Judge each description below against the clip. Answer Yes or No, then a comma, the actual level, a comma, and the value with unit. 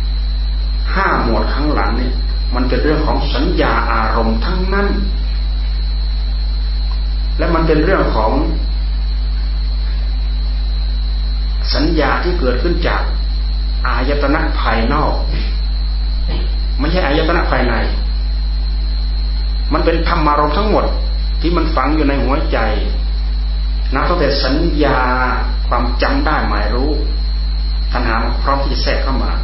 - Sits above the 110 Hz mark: No, very low, 75 Hz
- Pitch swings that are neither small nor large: No, wide, 9.0 semitones